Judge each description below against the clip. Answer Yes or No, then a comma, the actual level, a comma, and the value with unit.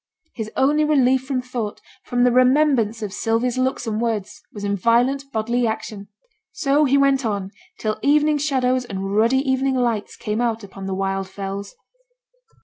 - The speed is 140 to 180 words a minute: Yes, average, 165 wpm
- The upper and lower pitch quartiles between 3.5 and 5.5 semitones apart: Yes, average, 4.0 semitones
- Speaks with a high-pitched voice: Yes, high, 240 Hz